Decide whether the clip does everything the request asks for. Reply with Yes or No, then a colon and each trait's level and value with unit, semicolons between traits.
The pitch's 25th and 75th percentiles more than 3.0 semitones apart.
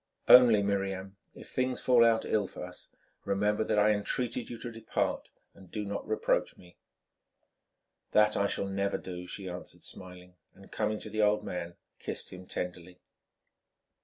No: average, 2.7 semitones